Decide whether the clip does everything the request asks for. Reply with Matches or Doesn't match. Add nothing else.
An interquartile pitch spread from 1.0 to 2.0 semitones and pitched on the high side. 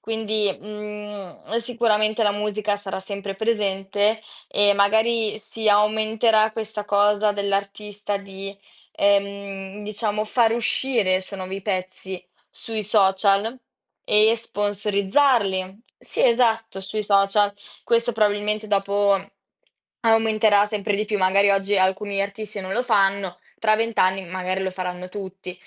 Matches